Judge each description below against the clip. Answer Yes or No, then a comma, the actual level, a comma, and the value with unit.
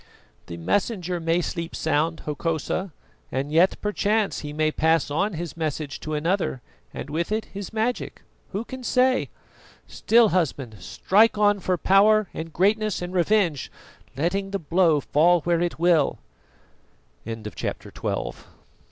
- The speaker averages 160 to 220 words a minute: No, average, 145 wpm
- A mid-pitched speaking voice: Yes, medium, 175 Hz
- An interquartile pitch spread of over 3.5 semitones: Yes, average, 4.7 semitones